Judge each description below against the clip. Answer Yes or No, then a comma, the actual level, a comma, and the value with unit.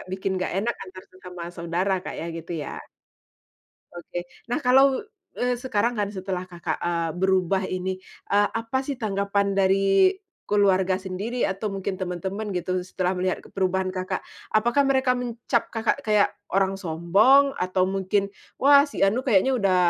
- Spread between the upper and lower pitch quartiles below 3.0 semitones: No, average, 3.7 semitones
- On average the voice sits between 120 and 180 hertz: No, high, 195 Hz